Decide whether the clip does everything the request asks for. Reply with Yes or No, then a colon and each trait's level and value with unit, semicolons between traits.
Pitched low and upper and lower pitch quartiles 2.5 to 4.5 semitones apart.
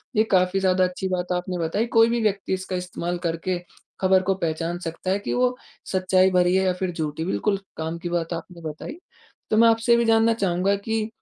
No: medium, 185 Hz; average, 2.8 semitones